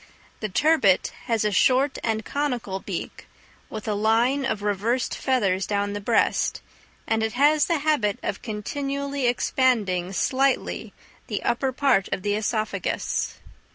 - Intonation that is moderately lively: Yes, average, 4.7 semitones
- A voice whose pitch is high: Yes, high, 225 Hz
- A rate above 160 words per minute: No, average, 140 wpm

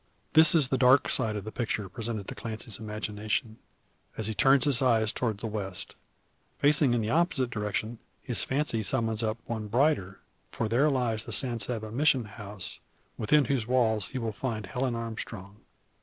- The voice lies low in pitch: Yes, low, 115 Hz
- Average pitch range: Yes, average, 3.2 semitones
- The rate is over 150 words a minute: Yes, average, 175 wpm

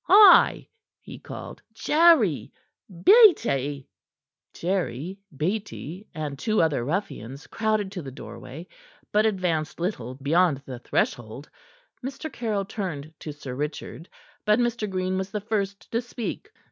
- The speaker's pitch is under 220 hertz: Yes, medium, 185 Hz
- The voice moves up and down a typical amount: No, wide, 6.6 semitones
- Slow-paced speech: Yes, slow, 125 wpm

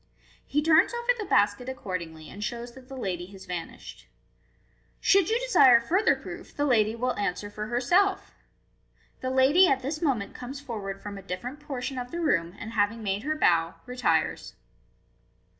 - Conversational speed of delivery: Yes, average, 175 wpm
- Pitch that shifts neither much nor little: No, wide, 6.3 semitones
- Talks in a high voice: Yes, high, 245 Hz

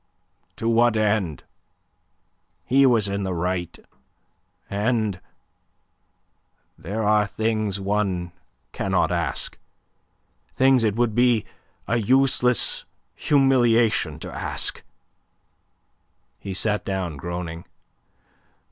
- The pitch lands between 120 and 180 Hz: No, low, 105 Hz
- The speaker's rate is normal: No, slow, 95 wpm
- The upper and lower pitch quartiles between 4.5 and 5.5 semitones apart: No, average, 4.0 semitones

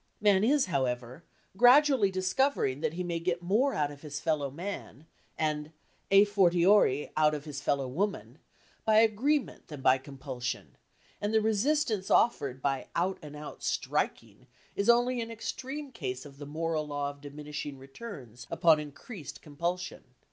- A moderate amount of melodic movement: No, wide, 6.6 semitones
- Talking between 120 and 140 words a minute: No, average, 155 wpm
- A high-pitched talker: No, medium, 165 Hz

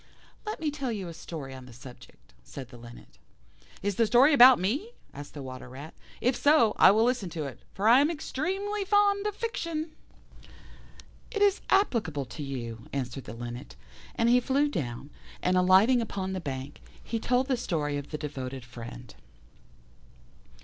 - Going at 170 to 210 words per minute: Yes, average, 175 wpm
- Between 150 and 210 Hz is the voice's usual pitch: Yes, medium, 185 Hz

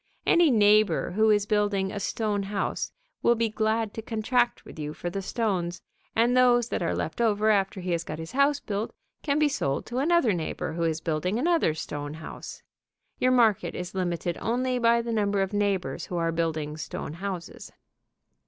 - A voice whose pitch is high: Yes, high, 205 Hz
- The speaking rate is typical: Yes, average, 190 wpm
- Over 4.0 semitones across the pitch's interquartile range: Yes, average, 5.2 semitones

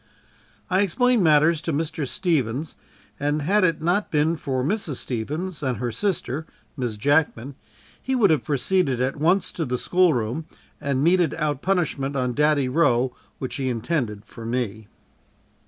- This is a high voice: No, medium, 150 Hz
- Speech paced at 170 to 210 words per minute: No, average, 160 wpm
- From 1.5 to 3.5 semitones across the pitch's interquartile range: No, average, 4.8 semitones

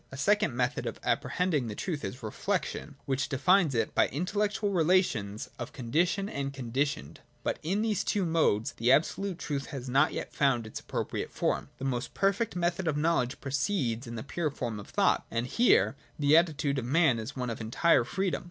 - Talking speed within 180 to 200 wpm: Yes, average, 190 wpm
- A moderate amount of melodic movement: No, wide, 6.3 semitones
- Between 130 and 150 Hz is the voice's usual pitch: Yes, medium, 140 Hz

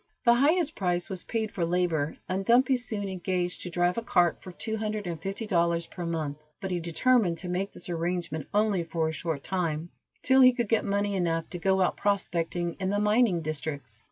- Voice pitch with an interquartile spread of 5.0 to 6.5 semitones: No, average, 3.7 semitones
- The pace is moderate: No, fast, 210 wpm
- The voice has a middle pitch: Yes, medium, 180 Hz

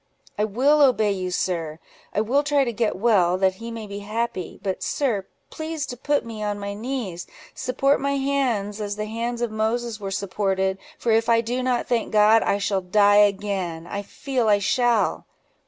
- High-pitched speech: Yes, high, 215 Hz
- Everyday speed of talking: Yes, average, 190 wpm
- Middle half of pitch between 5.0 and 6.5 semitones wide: No, average, 3.4 semitones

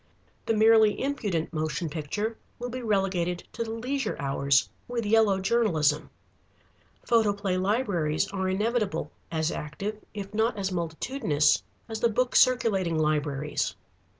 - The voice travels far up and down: Yes, wide, 5.9 semitones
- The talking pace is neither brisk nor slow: No, slow, 125 wpm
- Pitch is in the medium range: No, high, 200 Hz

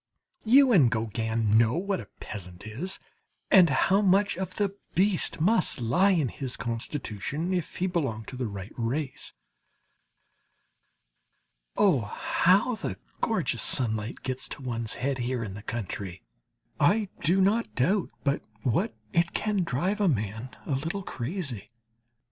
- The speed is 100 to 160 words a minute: Yes, average, 145 wpm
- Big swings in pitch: Yes, wide, 8.7 semitones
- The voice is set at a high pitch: No, medium, 140 Hz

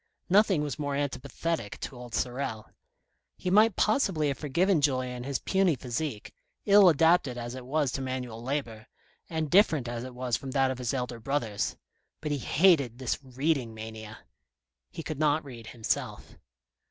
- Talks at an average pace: Yes, average, 165 wpm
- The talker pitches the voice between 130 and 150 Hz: Yes, low, 135 Hz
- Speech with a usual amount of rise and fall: Yes, average, 4.3 semitones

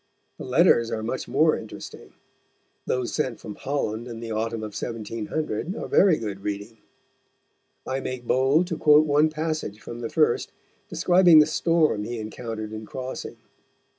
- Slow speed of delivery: No, average, 155 wpm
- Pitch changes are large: Yes, wide, 5.7 semitones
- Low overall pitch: Yes, low, 120 Hz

